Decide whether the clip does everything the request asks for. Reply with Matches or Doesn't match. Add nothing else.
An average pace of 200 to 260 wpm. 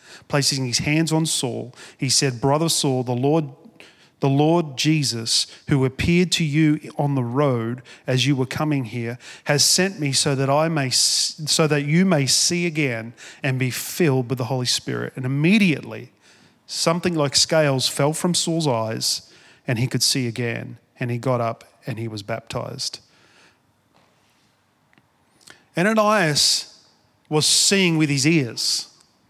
Doesn't match